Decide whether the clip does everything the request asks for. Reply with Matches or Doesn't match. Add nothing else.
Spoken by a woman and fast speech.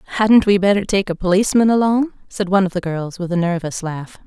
Matches